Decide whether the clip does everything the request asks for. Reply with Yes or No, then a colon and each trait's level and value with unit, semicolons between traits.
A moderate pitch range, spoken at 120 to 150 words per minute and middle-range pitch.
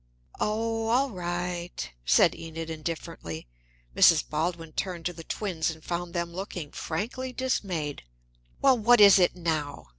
Yes: average, 4.4 semitones; average, 140 wpm; medium, 175 Hz